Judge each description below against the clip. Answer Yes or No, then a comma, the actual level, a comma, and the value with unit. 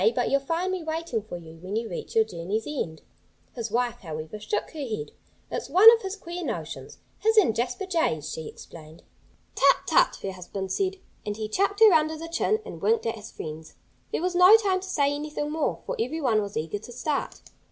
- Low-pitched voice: No, very high, 260 Hz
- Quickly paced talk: Yes, fast, 210 wpm